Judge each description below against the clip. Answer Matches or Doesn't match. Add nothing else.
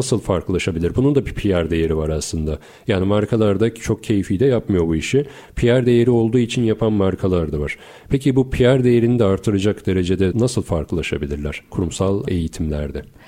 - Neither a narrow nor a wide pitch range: Doesn't match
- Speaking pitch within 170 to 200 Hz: Doesn't match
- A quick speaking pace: Matches